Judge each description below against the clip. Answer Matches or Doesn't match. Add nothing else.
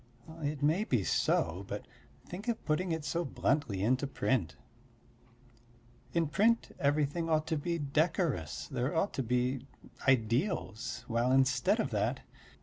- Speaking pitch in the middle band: Matches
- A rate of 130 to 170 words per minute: Matches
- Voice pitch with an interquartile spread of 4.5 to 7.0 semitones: Matches